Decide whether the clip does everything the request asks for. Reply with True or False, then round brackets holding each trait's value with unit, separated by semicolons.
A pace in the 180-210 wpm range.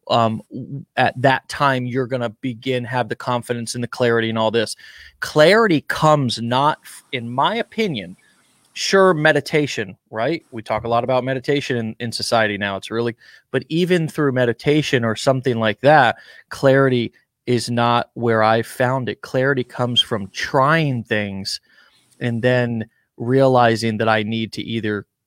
False (155 wpm)